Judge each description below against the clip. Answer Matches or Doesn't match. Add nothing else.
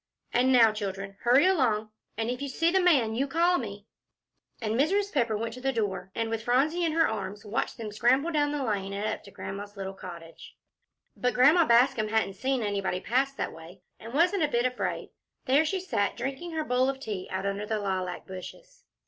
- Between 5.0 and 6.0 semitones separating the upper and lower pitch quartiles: Matches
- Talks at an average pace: Doesn't match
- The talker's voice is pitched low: Doesn't match